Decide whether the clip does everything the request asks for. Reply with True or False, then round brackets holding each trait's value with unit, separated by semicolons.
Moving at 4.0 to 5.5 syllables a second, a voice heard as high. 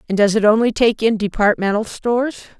False (5.8 syllables/s; 220 Hz)